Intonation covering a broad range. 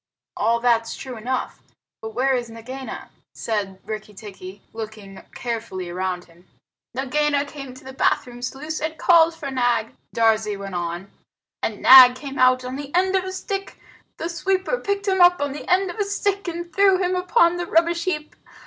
Yes: wide, 7.6 semitones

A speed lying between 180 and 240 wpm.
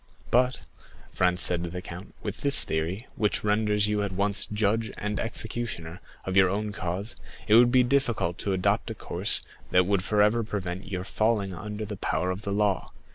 Yes: average, 185 wpm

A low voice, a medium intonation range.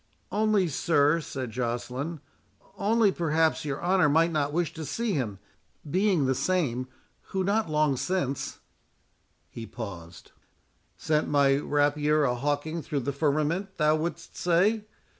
No: medium, 150 Hz; average, 4.0 semitones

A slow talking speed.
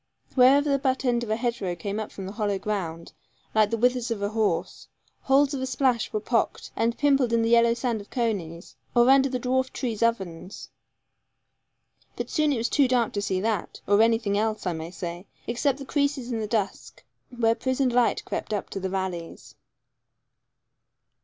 No: average, 185 wpm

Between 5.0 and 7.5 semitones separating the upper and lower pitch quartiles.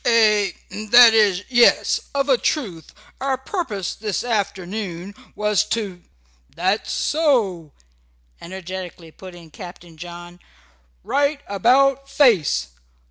Yes: wide, 5.6 semitones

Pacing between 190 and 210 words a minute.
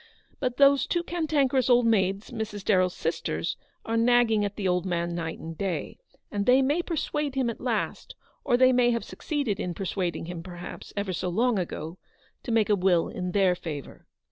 Yes: average, 195 wpm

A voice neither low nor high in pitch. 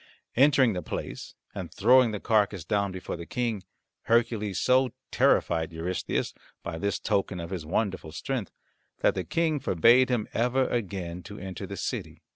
No: low, 100 Hz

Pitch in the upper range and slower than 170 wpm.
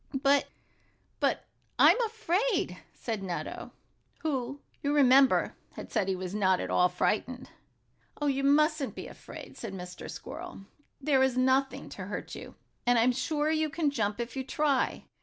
Yes: very high, 265 Hz; average, 155 wpm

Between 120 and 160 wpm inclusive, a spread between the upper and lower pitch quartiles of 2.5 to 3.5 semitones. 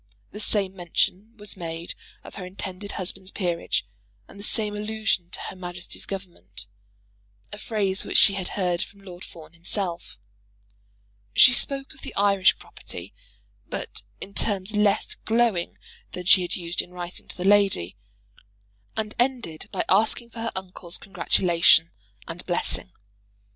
Yes: average, 150 wpm; average, 2.9 semitones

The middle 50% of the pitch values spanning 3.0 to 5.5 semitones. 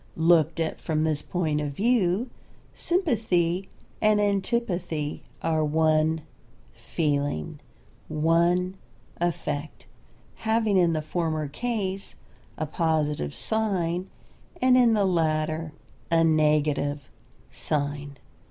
Yes: average, 3.8 semitones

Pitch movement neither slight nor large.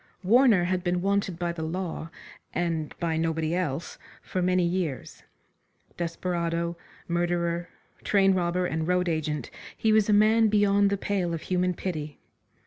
No: narrow, 2.3 semitones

